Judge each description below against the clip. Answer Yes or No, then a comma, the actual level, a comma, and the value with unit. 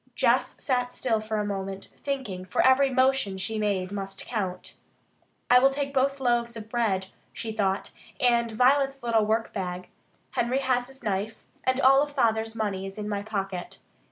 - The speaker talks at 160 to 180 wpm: Yes, average, 165 wpm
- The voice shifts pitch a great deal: No, average, 4.6 semitones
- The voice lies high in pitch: Yes, high, 225 Hz